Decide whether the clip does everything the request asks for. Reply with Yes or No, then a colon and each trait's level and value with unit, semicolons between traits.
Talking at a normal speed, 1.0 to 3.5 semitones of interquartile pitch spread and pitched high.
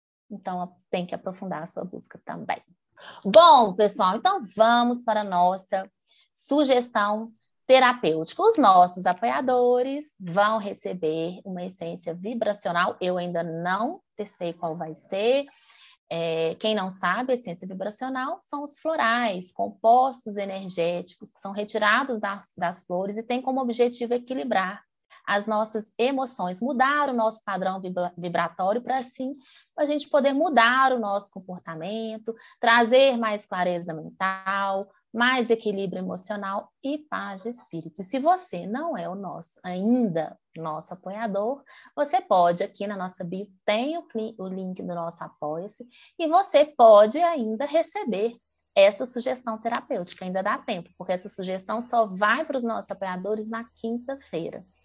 No: average, 140 wpm; average, 5.3 semitones; high, 215 Hz